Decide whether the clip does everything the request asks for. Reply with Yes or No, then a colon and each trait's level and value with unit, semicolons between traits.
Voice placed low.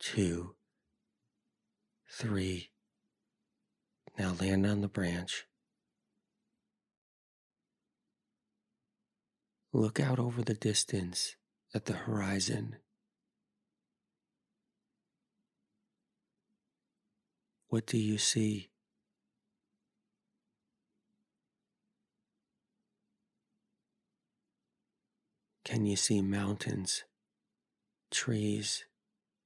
Yes: low, 120 Hz